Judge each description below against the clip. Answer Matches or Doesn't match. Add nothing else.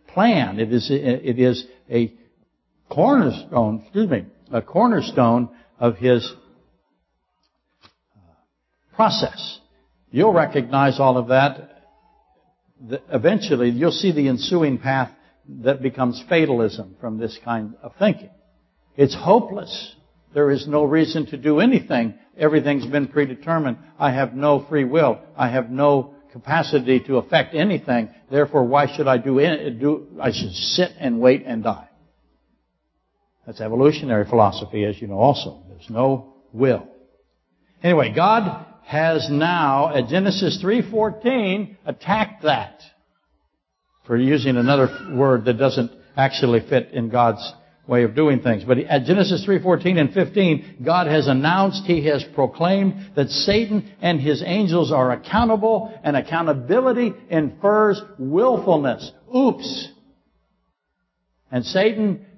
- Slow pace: Matches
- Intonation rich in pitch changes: Matches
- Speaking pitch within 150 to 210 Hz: Doesn't match